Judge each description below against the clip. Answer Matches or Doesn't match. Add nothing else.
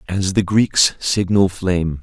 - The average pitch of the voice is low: Matches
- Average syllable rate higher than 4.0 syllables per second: Doesn't match